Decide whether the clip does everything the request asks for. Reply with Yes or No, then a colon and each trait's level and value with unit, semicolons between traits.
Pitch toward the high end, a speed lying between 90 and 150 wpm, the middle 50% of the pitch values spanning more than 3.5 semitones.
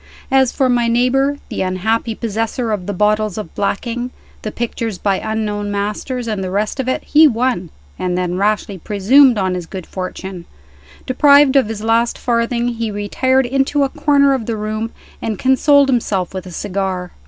No: high, 225 Hz; average, 175 wpm; average, 4.3 semitones